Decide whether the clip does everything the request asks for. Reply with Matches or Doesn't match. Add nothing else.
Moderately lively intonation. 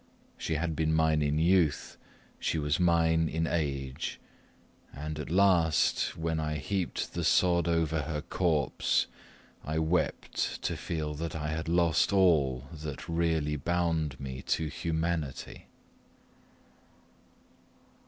Doesn't match